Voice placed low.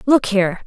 No: high, 215 Hz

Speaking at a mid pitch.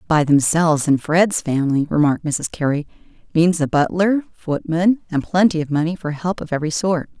Yes: medium, 160 Hz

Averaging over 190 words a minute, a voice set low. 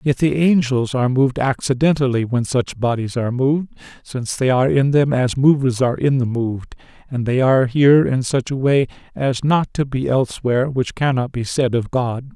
Yes: average, 200 wpm; low, 130 Hz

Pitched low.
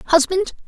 No: very high, 345 Hz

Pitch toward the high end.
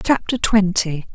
Yes: high, 200 Hz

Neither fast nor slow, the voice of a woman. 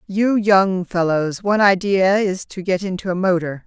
Yes: average, 180 wpm; female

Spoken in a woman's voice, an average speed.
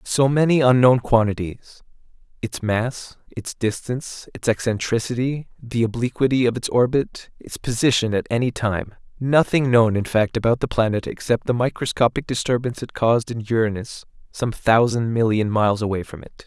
No: male; average, 150 wpm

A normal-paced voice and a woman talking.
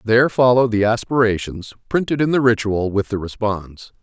No: average, 165 wpm; male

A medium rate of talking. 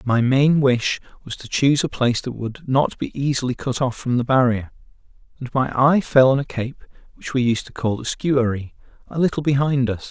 No: fast, 215 wpm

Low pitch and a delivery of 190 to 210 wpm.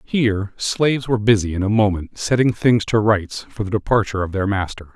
Yes: low, 105 Hz; fast, 205 wpm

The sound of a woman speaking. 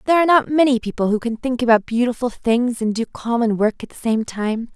Yes: female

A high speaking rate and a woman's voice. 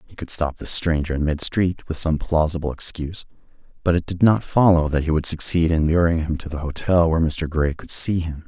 No: fast, 235 wpm; male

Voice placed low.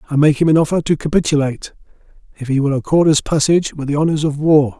No: medium, 150 Hz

